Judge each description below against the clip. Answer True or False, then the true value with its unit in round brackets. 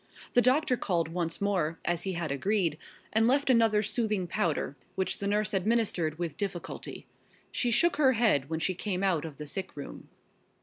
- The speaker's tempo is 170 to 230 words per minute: True (180 wpm)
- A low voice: False (190 Hz)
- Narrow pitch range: False (4.9 semitones)